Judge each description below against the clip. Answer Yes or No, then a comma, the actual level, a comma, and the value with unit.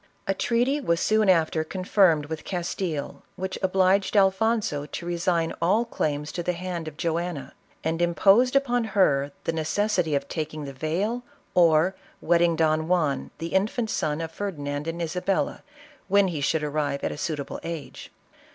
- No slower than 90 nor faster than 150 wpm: No, average, 165 wpm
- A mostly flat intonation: No, average, 3.7 semitones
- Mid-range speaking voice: Yes, medium, 170 Hz